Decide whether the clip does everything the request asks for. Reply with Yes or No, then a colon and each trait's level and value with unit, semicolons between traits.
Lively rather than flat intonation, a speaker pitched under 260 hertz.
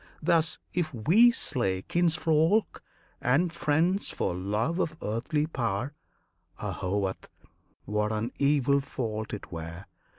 Yes: wide, 7.4 semitones; low, 135 Hz